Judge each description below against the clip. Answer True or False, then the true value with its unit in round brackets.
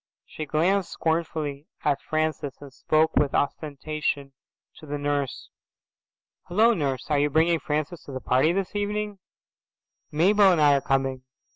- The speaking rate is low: False (145 wpm)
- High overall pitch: False (155 Hz)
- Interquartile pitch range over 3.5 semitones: False (3.2 semitones)